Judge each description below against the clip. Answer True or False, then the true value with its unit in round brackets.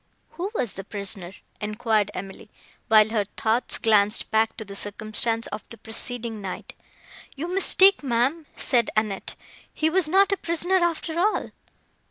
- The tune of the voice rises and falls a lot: True (7.5 semitones)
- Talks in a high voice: True (230 Hz)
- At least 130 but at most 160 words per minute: True (150 wpm)